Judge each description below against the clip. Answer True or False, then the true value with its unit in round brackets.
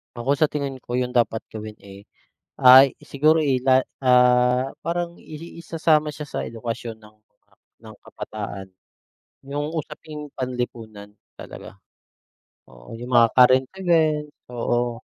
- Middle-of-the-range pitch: False (125 Hz)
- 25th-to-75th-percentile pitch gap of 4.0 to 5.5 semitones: True (4.3 semitones)